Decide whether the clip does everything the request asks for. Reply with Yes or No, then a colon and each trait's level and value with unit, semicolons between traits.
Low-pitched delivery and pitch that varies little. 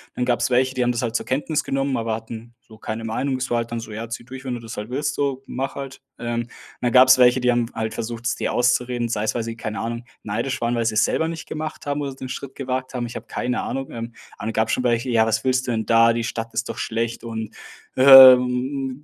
Yes: low, 120 Hz; narrow, 2.2 semitones